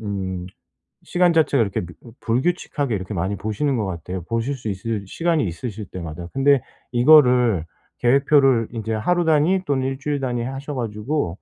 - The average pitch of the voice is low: Yes, low, 120 Hz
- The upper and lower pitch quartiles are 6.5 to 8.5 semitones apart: No, wide, 5.7 semitones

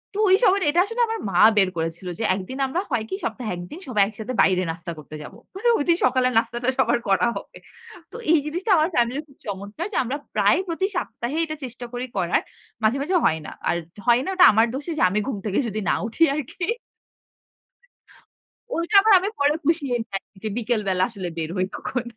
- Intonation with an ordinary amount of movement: No, wide, 7.8 semitones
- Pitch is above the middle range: Yes, high, 245 Hz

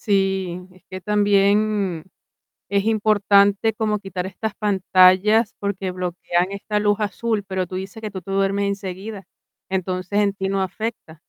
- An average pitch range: No, narrow, 1.9 semitones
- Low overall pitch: No, high, 195 Hz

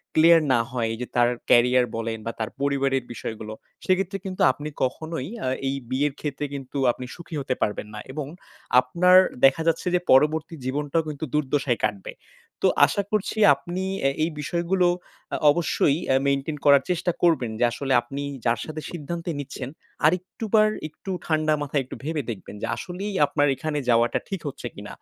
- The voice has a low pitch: No, medium, 145 Hz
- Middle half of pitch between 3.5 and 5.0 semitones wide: Yes, average, 4.4 semitones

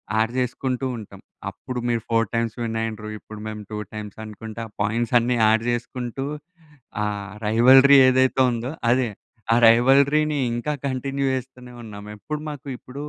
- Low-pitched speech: Yes, low, 120 Hz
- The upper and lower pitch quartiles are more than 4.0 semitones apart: No, average, 2.9 semitones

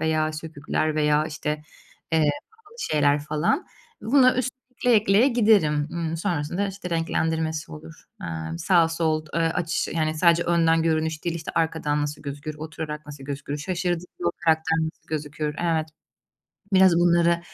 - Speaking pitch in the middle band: Yes, medium, 160 Hz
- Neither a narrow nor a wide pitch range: No, narrow, 2.2 semitones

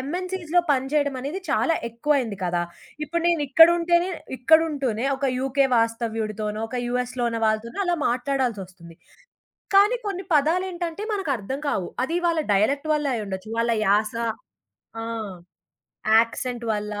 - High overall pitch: Yes, very high, 265 Hz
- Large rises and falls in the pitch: Yes, wide, 6.3 semitones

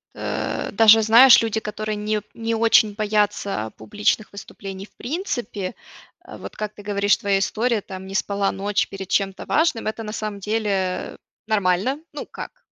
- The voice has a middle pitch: No, high, 210 Hz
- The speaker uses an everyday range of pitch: No, narrow, 2.1 semitones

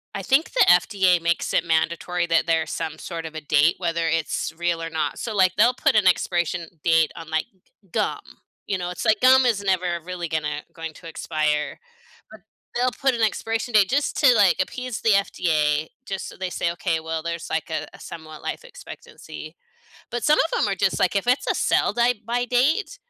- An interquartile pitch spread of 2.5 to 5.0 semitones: No, wide, 5.5 semitones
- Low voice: No, medium, 180 Hz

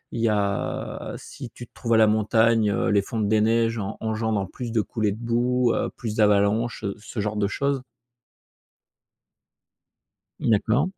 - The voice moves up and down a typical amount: No, narrow, 1.8 semitones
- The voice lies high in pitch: No, low, 110 Hz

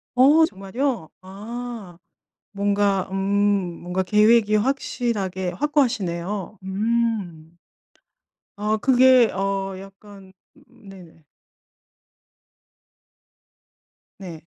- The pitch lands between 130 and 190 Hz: No, high, 200 Hz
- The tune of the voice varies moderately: Yes, average, 3.8 semitones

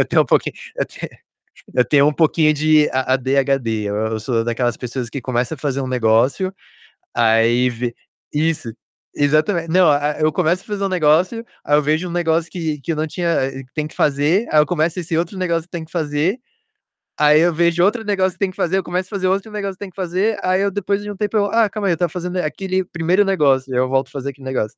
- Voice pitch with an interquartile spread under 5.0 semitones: No, average, 5.3 semitones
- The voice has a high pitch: No, medium, 160 Hz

